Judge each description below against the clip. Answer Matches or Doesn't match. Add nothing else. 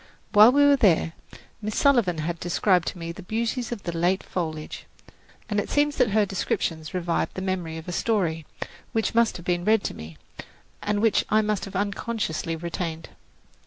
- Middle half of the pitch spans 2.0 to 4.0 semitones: Doesn't match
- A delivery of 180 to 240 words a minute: Matches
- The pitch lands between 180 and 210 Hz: Matches